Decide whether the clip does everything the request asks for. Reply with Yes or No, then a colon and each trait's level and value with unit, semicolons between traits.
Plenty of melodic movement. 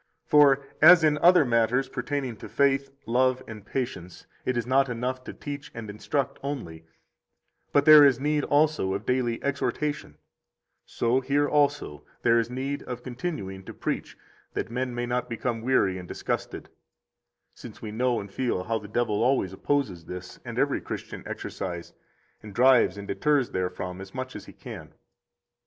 No: average, 4.8 semitones